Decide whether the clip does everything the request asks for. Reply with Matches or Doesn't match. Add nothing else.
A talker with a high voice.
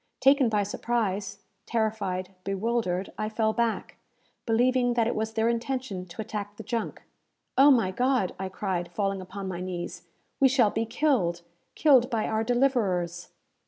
Matches